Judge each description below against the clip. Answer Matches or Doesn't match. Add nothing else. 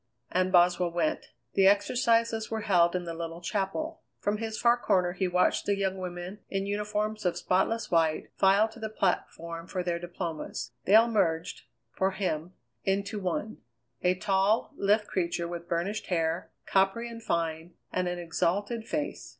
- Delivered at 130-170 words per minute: Matches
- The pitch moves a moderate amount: Matches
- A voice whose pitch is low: Doesn't match